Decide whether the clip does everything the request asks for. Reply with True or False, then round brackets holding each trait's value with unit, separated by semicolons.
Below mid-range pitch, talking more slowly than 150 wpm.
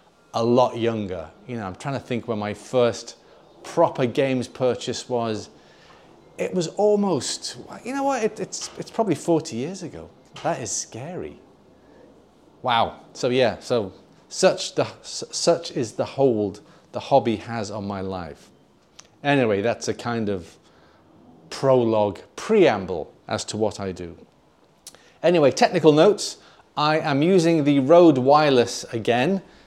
True (120 Hz; 140 wpm)